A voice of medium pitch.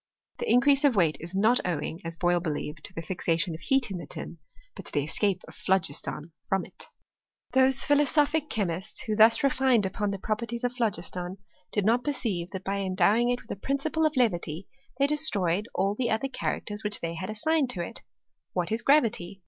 No: high, 210 Hz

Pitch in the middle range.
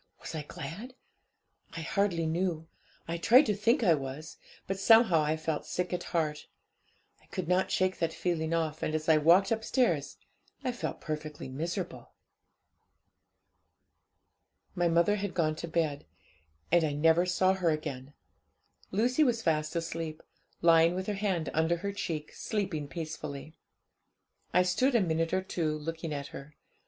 Yes: medium, 165 Hz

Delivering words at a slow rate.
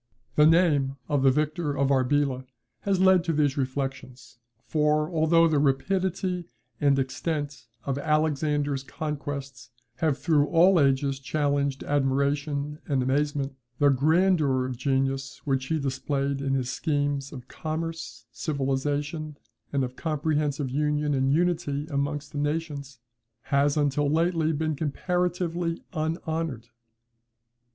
Yes: slow, 120 wpm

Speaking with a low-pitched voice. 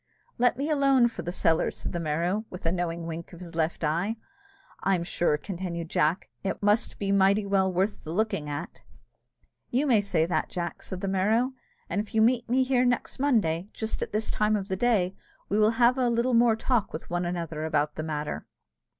No: high, 195 Hz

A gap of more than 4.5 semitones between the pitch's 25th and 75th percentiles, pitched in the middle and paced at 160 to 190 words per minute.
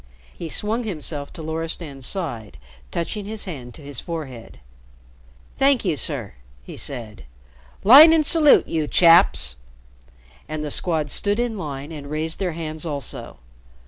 No: wide, 5.5 semitones; medium, 160 Hz; average, 145 wpm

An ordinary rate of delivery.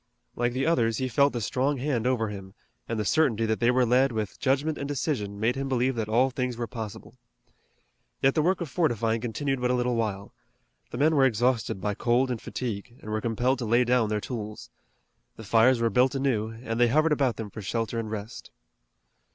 No: fast, 215 wpm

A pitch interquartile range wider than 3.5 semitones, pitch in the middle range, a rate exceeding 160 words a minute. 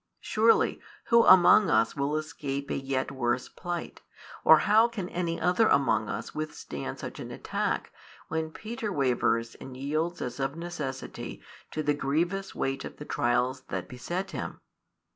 No: average, 4.9 semitones; medium, 155 Hz; average, 155 wpm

